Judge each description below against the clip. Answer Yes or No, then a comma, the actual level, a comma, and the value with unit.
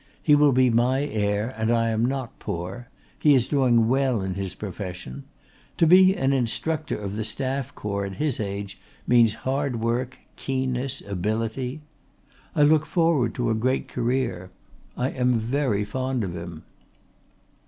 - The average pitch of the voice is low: Yes, low, 120 Hz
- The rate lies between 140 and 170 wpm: Yes, average, 155 wpm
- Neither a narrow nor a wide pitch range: Yes, average, 4.3 semitones